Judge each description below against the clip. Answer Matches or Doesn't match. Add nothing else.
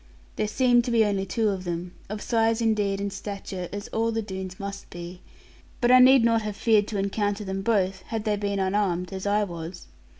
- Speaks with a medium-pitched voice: Doesn't match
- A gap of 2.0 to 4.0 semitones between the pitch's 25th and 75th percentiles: Matches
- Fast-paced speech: Matches